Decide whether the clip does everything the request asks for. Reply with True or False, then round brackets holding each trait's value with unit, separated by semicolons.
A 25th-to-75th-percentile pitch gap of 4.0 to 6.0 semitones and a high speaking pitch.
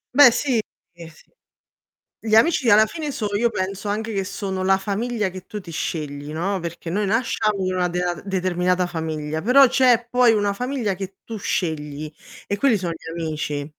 True (4.6 semitones; 195 Hz)